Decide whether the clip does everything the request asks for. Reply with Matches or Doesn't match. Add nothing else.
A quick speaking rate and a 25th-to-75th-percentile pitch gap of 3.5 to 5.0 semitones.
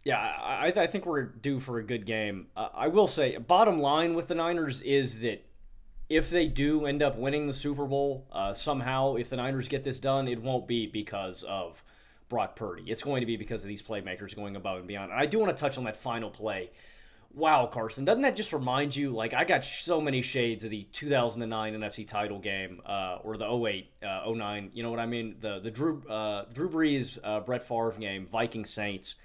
Matches